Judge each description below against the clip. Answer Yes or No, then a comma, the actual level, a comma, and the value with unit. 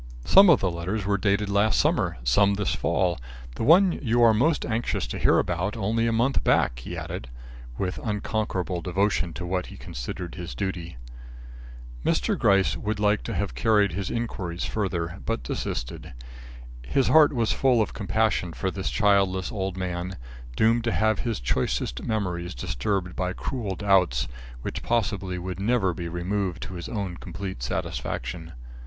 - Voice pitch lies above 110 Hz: No, very low, 95 Hz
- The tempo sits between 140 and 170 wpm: Yes, average, 165 wpm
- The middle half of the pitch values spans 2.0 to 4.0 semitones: Yes, average, 3.7 semitones